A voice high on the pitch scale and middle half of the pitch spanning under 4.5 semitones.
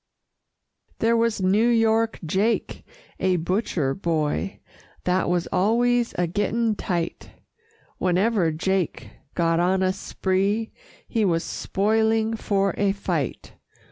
Yes: high, 195 Hz; average, 3.9 semitones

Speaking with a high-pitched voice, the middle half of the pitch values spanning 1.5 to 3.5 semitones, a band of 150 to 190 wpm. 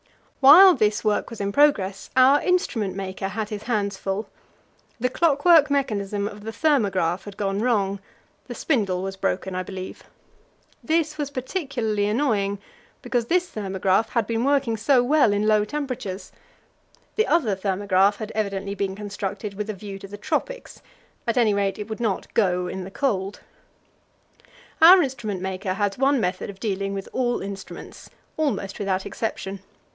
No: high, 210 Hz; average, 4.7 semitones; average, 160 wpm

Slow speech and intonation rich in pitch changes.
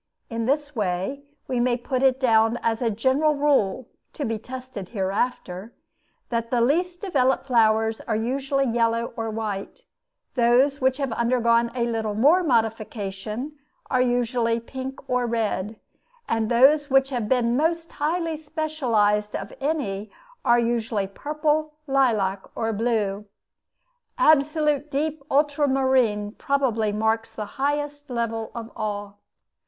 No: slow, 130 wpm; average, 4.0 semitones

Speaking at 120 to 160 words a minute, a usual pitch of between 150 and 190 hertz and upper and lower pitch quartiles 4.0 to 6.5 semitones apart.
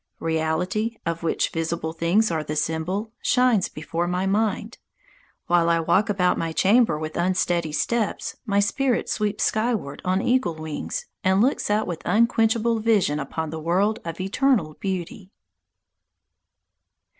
Yes: average, 140 wpm; medium, 185 Hz; average, 4.9 semitones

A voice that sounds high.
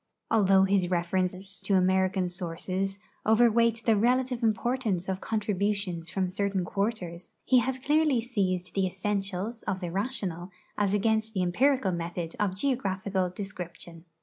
Yes: high, 195 Hz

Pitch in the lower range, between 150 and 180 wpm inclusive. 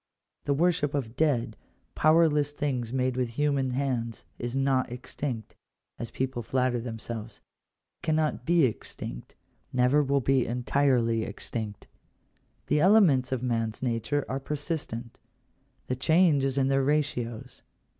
No: low, 130 Hz; slow, 135 wpm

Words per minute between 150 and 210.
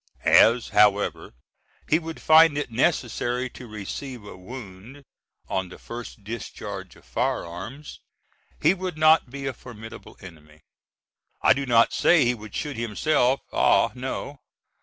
No: average, 140 wpm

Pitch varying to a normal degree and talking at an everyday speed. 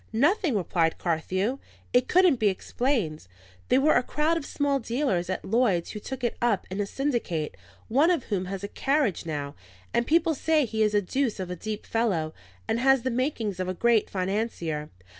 No: wide, 6.5 semitones; average, 190 wpm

